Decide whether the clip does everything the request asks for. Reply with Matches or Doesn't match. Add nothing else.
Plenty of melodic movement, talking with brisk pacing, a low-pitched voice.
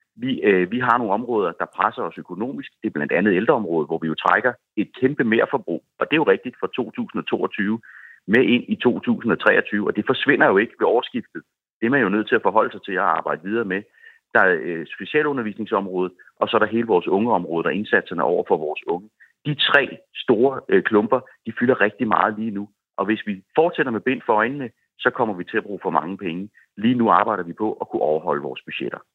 Matches